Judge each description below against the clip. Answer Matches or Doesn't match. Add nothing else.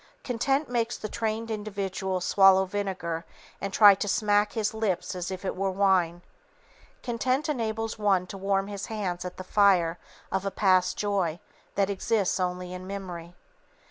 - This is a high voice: Matches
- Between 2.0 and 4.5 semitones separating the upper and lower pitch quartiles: Matches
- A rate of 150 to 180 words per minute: Matches